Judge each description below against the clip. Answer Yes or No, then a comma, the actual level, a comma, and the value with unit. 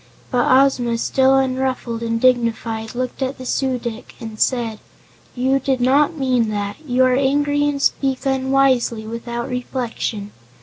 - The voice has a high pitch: Yes, very high, 255 Hz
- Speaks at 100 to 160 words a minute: Yes, average, 145 wpm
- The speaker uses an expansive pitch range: No, narrow, 2.5 semitones